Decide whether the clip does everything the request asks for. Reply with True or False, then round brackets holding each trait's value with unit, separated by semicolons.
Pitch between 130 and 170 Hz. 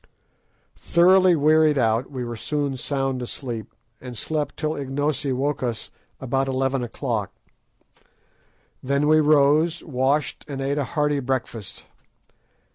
True (140 Hz)